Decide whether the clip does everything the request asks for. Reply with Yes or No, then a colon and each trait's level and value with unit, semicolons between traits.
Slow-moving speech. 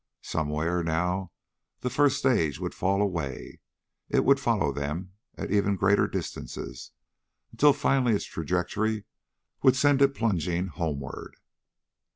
Yes: slow, 125 wpm